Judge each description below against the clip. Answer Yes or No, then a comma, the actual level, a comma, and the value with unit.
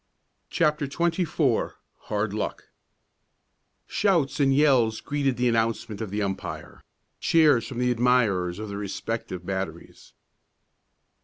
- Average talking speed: No, slow, 110 wpm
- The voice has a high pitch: No, low, 120 Hz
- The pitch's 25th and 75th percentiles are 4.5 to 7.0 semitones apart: Yes, wide, 5.4 semitones